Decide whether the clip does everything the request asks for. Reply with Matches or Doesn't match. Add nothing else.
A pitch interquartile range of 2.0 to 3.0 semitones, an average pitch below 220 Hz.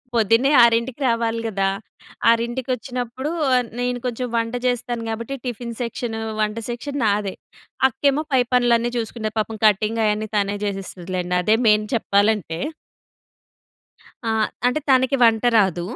Doesn't match